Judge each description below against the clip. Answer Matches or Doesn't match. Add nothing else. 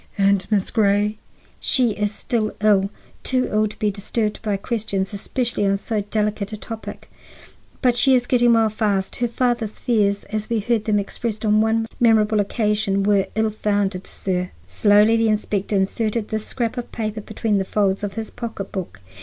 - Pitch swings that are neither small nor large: Doesn't match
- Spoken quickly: Doesn't match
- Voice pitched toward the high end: Matches